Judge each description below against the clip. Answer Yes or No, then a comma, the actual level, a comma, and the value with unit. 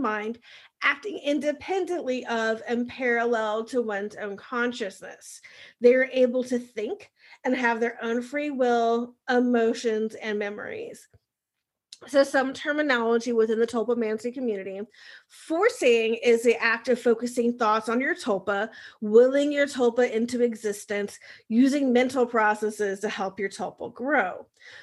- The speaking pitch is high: Yes, high, 235 Hz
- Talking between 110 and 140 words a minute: Yes, slow, 135 wpm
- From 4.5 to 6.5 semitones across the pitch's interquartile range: No, narrow, 2.5 semitones